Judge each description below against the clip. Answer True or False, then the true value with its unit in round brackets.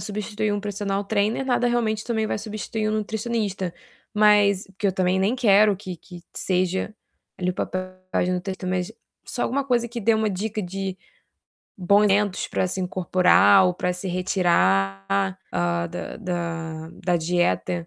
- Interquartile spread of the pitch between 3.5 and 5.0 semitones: False (3.0 semitones)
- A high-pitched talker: True (195 Hz)